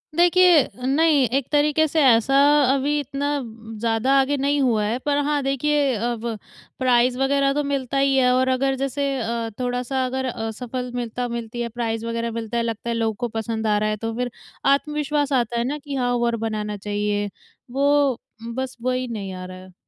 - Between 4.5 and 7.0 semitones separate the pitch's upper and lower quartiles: No, average, 3.4 semitones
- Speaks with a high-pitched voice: Yes, very high, 250 Hz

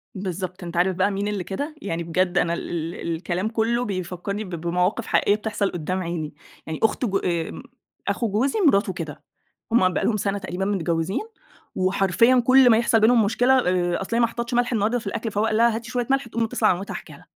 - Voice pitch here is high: Yes, high, 200 Hz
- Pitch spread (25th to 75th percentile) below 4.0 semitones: No, average, 4.3 semitones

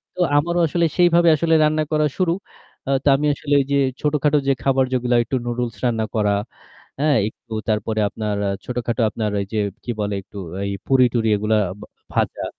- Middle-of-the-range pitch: No, low, 125 Hz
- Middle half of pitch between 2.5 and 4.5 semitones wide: No, wide, 5.4 semitones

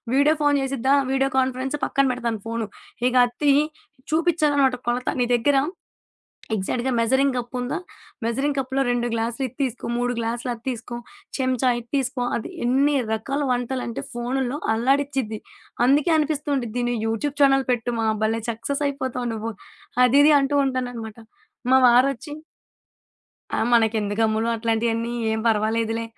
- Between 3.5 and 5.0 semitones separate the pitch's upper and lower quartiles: No, average, 3.0 semitones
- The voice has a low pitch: No, very high, 250 Hz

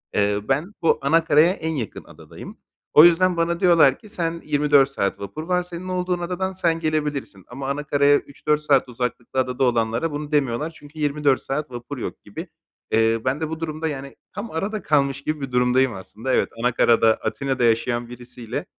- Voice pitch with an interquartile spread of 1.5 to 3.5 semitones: No, average, 4.7 semitones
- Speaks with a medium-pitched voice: Yes, medium, 145 Hz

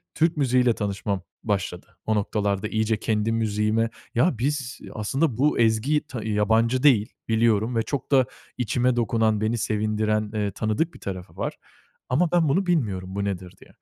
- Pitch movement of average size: Yes, average, 3.3 semitones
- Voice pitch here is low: Yes, low, 110 Hz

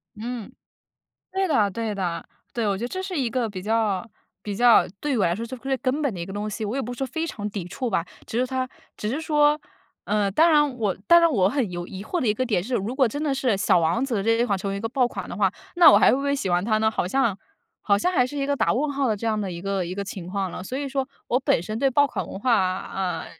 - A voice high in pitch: Yes, high, 230 Hz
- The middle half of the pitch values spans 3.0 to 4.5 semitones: No, average, 5.3 semitones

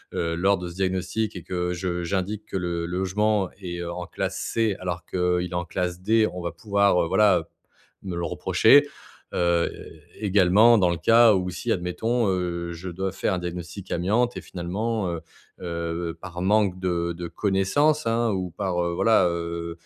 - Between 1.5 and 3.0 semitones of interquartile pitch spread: Yes, average, 2.7 semitones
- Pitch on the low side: Yes, very low, 90 Hz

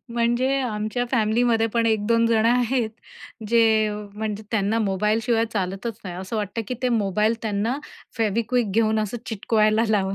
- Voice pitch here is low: No, high, 220 Hz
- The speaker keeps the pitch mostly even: Yes, narrow, 1.8 semitones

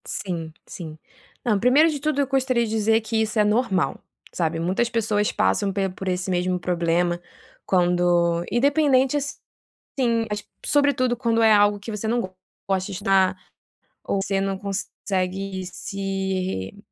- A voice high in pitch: Yes, high, 200 Hz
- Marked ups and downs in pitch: No, average, 4.2 semitones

